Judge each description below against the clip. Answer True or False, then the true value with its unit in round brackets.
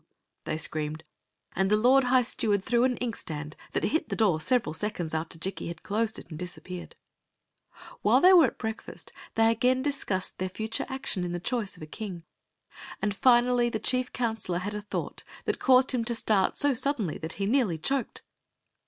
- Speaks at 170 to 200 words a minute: True (190 wpm)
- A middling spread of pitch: False (5.7 semitones)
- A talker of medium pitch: False (220 Hz)